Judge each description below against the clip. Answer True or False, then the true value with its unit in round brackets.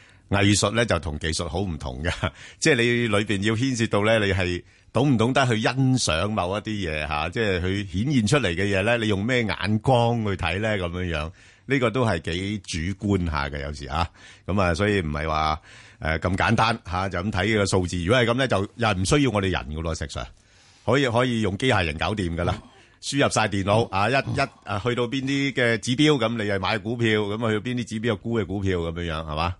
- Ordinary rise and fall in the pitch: True (4.6 semitones)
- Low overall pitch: True (100 Hz)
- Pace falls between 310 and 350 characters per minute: True (320 characters per minute)